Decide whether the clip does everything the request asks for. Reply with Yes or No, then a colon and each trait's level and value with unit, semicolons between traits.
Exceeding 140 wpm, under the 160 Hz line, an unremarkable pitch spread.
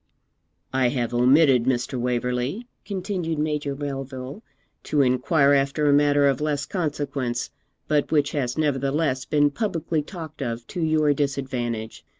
No: slow, 135 wpm; medium, 140 Hz; average, 3.0 semitones